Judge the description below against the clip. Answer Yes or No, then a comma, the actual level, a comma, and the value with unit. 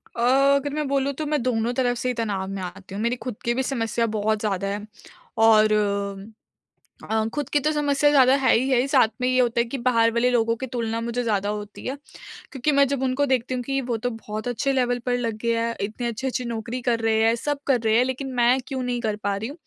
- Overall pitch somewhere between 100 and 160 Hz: No, high, 240 Hz